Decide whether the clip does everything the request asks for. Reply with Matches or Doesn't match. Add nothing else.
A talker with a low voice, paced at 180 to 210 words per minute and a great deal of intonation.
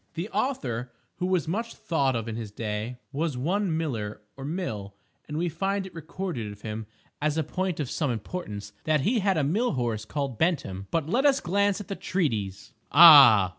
Doesn't match